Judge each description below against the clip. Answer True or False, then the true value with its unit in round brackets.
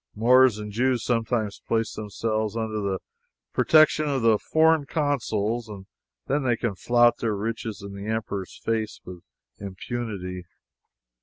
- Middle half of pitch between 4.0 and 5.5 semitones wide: False (2.8 semitones)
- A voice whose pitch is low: True (110 Hz)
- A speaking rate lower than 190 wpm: True (140 wpm)